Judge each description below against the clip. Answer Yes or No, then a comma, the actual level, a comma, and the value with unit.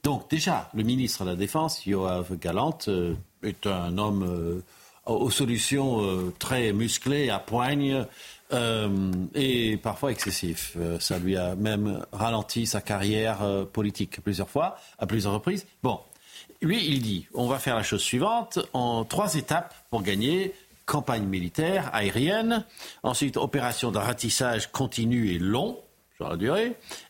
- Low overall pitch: Yes, low, 115 Hz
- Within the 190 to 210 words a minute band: No, average, 150 wpm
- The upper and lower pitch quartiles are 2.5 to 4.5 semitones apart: No, wide, 5.6 semitones